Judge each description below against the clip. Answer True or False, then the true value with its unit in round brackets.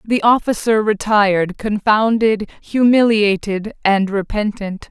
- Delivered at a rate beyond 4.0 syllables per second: False (3.9 syllables/s)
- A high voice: True (210 Hz)